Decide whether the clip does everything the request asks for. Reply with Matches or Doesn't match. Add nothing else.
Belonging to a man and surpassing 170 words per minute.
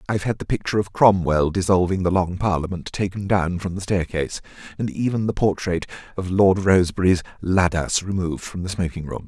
Matches